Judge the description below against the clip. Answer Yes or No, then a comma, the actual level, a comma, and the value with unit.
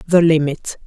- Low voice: No, medium, 160 Hz